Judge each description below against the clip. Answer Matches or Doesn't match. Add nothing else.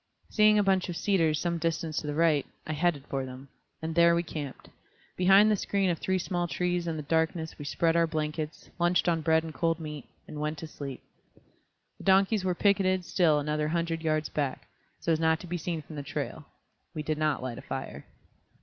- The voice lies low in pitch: Doesn't match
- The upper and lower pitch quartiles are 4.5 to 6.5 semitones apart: Doesn't match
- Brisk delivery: Matches